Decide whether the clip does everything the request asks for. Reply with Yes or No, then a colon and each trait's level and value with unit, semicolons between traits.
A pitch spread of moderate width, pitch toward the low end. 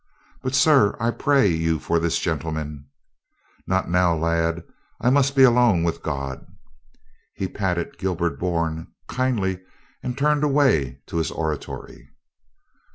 No: wide, 7.4 semitones; very low, 90 Hz